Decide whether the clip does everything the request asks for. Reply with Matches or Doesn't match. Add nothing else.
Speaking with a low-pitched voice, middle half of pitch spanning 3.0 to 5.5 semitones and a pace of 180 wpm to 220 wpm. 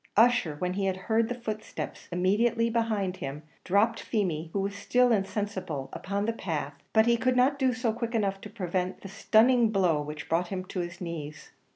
Doesn't match